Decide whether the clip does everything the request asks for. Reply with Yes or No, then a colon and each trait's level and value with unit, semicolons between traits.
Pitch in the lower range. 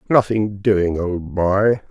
Yes: low, 100 Hz